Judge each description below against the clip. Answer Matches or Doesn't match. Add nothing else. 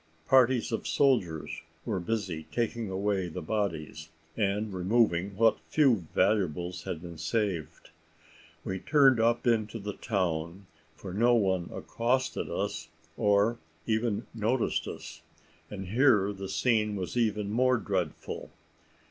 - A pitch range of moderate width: Matches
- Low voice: Matches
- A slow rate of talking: Matches